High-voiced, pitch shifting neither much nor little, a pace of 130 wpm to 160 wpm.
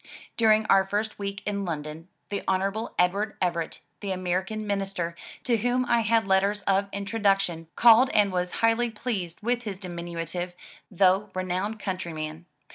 Yes: high, 195 Hz; average, 3.2 semitones; average, 150 wpm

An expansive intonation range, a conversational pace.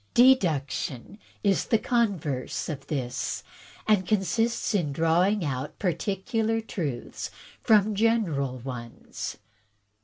No: wide, 7.4 semitones; slow, 100 wpm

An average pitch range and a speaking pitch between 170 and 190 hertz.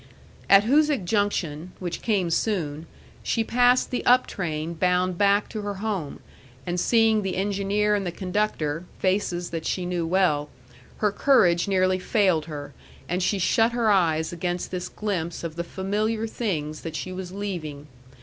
Yes: average, 3.6 semitones; medium, 185 Hz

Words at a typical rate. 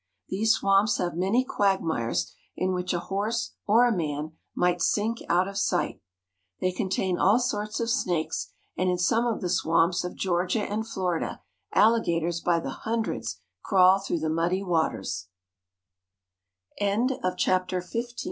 No: slow, 130 wpm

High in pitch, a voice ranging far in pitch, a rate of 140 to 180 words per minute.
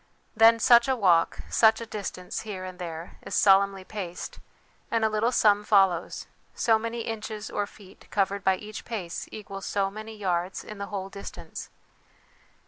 No: high, 205 Hz; narrow, 2.5 semitones; average, 165 wpm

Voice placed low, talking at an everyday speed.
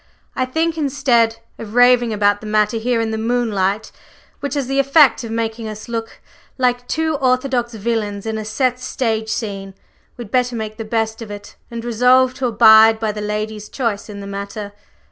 No: high, 225 Hz; average, 185 wpm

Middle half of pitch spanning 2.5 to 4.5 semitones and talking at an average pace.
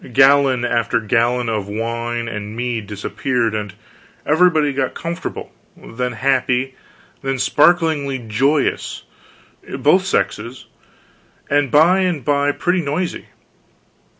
No: average, 3.8 semitones; slow, 105 wpm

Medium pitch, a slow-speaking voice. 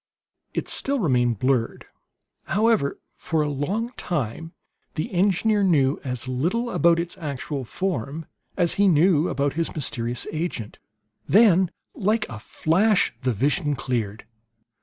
Yes: medium, 160 Hz; slow, 130 wpm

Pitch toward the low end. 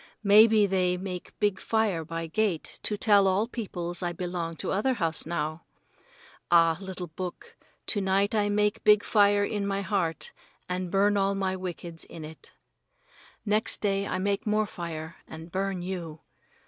No: high, 190 Hz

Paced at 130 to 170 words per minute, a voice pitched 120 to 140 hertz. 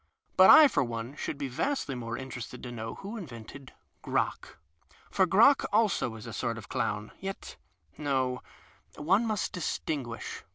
Yes: average, 155 wpm; low, 135 Hz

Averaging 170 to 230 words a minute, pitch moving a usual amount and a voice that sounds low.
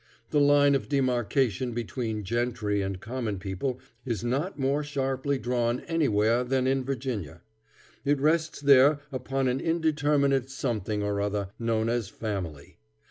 No: slow, 135 wpm; average, 4.0 semitones; low, 125 Hz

